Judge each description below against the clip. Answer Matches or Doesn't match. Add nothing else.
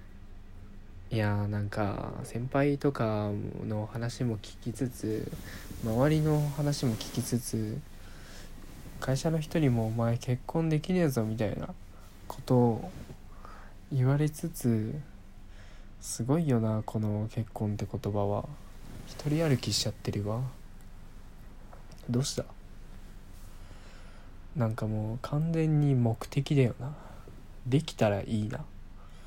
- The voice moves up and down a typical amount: Matches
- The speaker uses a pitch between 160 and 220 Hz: Doesn't match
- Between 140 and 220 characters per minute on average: Matches